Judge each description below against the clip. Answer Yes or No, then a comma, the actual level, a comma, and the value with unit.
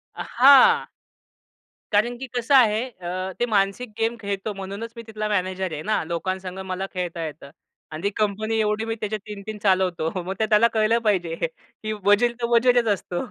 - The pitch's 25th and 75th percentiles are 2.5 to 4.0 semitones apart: Yes, average, 3.3 semitones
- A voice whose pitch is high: Yes, high, 210 Hz